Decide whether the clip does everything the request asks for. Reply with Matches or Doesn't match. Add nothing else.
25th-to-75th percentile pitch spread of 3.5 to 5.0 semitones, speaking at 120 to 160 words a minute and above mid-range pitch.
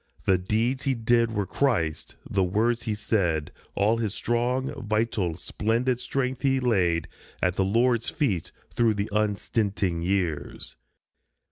Doesn't match